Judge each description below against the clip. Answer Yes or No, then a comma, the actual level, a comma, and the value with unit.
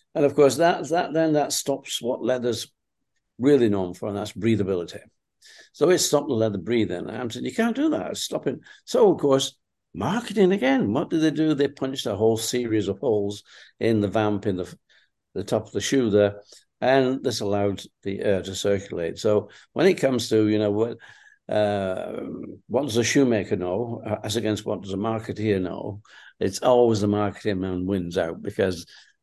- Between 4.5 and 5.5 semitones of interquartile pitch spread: Yes, average, 5.1 semitones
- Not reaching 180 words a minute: No, average, 190 wpm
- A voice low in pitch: Yes, low, 115 Hz